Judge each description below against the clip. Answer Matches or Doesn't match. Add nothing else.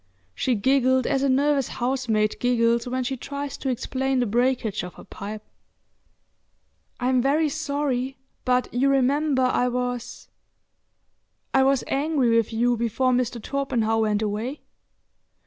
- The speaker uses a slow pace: Matches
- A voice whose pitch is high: Matches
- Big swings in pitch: Doesn't match